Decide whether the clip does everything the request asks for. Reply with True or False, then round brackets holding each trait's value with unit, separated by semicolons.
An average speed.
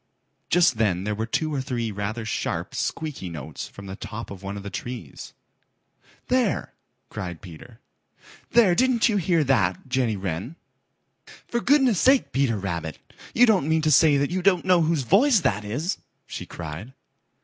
True (165 wpm)